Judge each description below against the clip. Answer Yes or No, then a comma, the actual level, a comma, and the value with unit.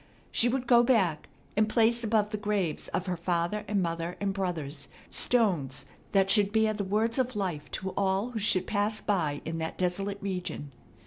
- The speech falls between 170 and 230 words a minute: Yes, average, 185 wpm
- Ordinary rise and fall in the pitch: Yes, average, 3.6 semitones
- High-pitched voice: Yes, high, 200 Hz